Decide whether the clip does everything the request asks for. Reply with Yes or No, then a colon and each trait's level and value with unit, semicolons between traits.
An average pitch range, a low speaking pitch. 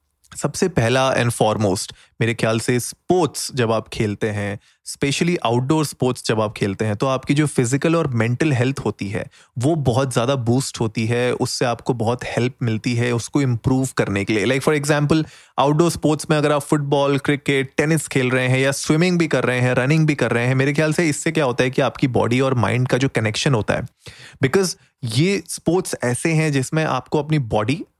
Yes: average, 4.2 semitones; low, 130 Hz